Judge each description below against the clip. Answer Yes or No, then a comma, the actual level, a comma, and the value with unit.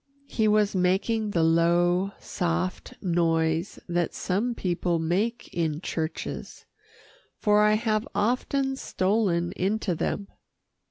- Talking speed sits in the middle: No, slow, 110 wpm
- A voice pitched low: No, medium, 185 Hz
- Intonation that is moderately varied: Yes, average, 3.9 semitones